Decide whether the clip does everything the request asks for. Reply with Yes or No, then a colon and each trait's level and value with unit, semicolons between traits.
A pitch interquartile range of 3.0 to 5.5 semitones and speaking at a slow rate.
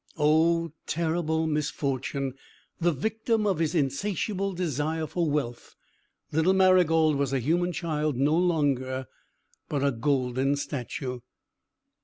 Yes: average, 3.6 semitones; slow, 115 wpm